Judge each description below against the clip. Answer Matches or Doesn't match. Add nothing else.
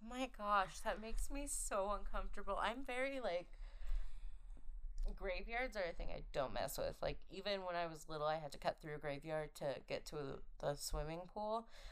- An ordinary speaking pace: Matches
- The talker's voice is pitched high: Matches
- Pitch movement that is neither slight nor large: Doesn't match